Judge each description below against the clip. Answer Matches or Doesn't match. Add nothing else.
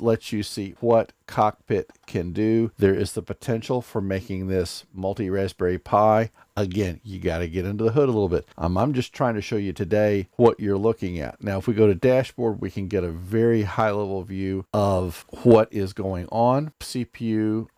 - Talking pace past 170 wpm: Matches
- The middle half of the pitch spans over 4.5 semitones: Doesn't match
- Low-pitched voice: Matches